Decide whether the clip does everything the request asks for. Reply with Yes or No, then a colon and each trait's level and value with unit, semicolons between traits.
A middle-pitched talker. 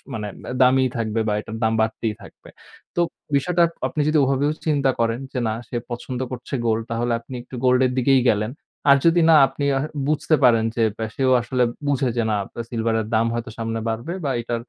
No: low, 120 Hz